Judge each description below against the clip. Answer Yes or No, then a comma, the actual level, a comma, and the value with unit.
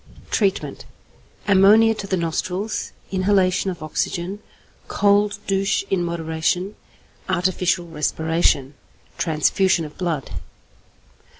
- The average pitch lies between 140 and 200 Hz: Yes, medium, 185 Hz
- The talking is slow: Yes, slow, 90 wpm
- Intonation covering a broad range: No, average, 3.1 semitones